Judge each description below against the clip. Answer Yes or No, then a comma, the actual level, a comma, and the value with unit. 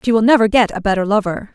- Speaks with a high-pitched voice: Yes, high, 215 Hz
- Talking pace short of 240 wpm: No, fast, 270 wpm